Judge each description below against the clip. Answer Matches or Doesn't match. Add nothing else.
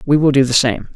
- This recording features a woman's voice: Doesn't match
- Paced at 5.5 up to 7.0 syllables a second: Matches